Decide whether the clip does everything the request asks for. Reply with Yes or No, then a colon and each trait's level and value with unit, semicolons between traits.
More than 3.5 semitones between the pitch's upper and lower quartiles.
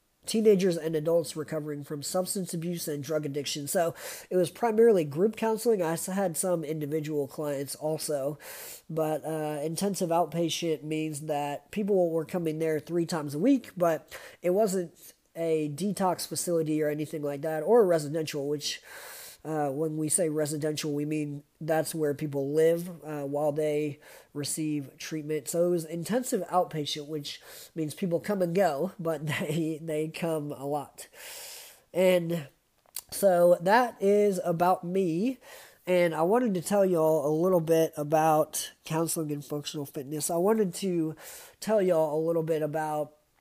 No: average, 2.9 semitones